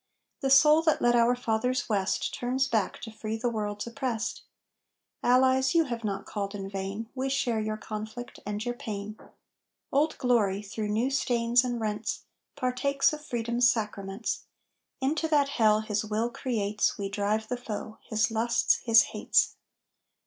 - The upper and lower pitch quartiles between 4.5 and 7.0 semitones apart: No, average, 3.0 semitones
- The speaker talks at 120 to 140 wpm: No, average, 155 wpm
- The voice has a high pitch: Yes, high, 230 Hz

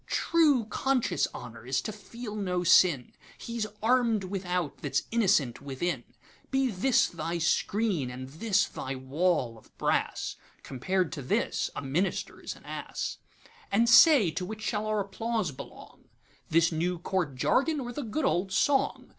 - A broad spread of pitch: Yes, wide, 6.5 semitones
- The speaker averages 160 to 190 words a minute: No, average, 140 wpm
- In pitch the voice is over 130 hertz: Yes, high, 190 Hz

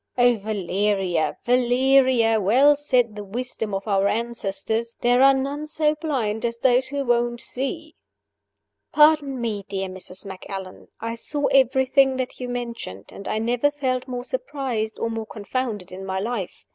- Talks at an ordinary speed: Yes, average, 155 wpm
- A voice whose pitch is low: No, high, 240 Hz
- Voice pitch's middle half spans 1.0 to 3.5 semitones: No, average, 4.1 semitones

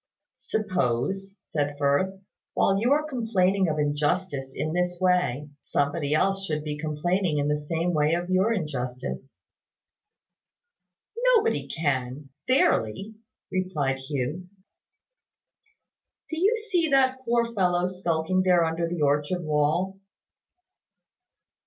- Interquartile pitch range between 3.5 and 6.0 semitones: Yes, average, 4.6 semitones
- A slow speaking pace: Yes, slow, 115 wpm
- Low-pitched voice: No, medium, 170 Hz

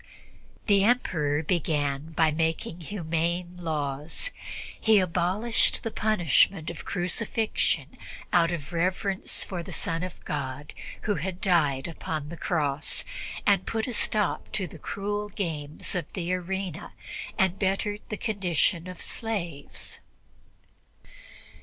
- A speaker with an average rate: No, slow, 120 wpm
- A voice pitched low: No, medium, 175 Hz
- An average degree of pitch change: Yes, average, 3.8 semitones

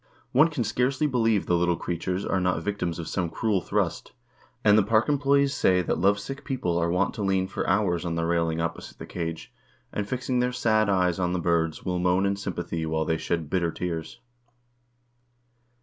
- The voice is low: Yes, very low, 95 Hz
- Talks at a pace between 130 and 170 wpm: No, average, 195 wpm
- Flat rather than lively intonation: No, average, 4.3 semitones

